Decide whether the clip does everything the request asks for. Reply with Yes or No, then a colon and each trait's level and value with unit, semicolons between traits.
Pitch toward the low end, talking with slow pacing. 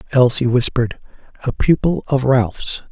Yes: low, 125 Hz; slow, 125 wpm